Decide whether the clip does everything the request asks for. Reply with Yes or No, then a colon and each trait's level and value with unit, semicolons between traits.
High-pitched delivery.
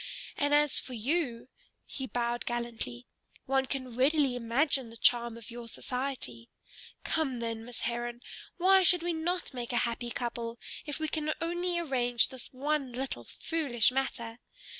Yes: very high, 250 Hz